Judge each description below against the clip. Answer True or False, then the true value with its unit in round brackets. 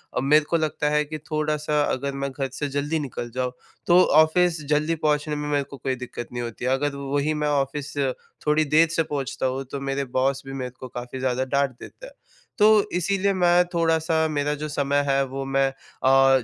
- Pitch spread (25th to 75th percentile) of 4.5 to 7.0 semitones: False (2.4 semitones)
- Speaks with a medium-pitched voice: True (145 Hz)